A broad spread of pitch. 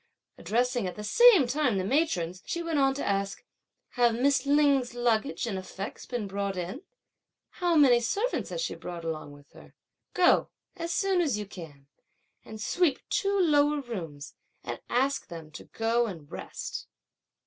Yes: wide, 7.2 semitones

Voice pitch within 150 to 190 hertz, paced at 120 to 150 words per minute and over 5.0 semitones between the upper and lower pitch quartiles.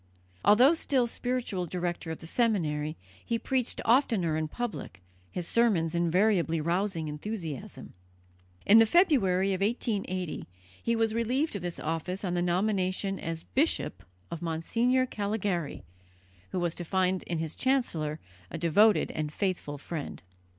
Yes: medium, 185 Hz; average, 140 wpm; wide, 5.4 semitones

